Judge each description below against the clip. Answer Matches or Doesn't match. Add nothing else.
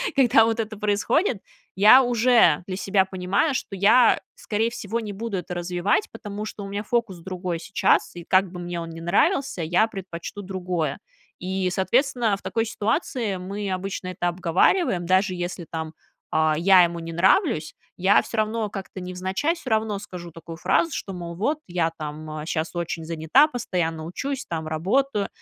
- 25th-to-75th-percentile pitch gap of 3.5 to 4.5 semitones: Matches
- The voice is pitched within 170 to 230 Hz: Matches